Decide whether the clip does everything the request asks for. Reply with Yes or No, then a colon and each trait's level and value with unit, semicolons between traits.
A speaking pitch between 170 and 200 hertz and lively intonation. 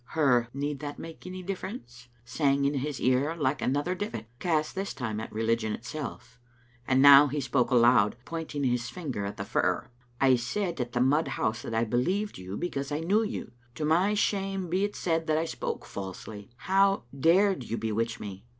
No: medium, 140 Hz; wide, 5.8 semitones